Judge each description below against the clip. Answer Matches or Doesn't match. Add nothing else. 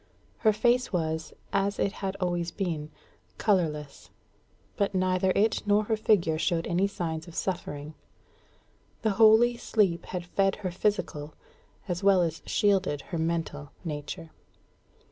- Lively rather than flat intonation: Doesn't match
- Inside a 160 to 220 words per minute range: Doesn't match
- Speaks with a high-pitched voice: Doesn't match